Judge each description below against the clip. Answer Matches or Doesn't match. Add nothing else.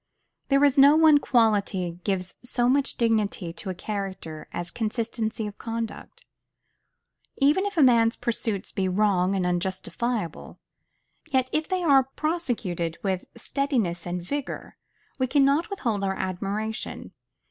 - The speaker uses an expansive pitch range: Matches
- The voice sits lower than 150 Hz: Doesn't match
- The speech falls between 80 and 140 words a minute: Matches